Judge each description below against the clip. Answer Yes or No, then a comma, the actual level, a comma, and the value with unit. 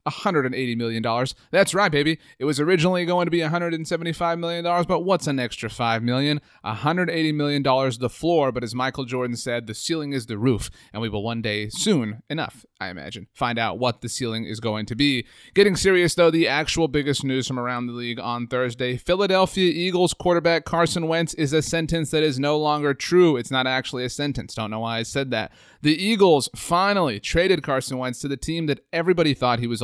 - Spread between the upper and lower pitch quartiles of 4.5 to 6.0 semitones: Yes, wide, 5.5 semitones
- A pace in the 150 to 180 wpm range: No, fast, 205 wpm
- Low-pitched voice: No, medium, 145 Hz